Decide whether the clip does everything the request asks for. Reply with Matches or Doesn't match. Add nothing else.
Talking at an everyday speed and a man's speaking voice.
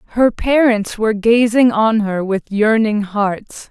Doesn't match